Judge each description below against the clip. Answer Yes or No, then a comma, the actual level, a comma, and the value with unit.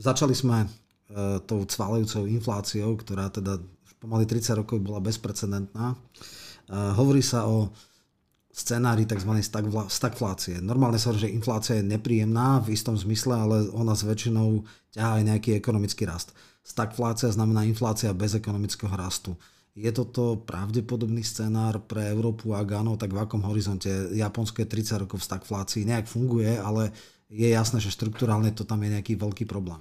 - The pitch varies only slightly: Yes, narrow, 1.9 semitones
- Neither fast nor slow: Yes, average, 150 wpm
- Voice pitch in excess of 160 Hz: No, low, 110 Hz